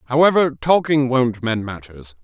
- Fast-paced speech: No, slow, 135 wpm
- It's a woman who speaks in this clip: No, male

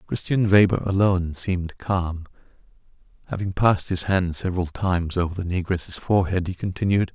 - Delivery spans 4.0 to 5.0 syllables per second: No, 5.5 syllables/s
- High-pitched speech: No, very low, 90 Hz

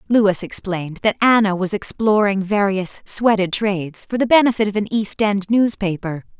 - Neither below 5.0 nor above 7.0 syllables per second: No, 4.8 syllables/s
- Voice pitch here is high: Yes, high, 205 Hz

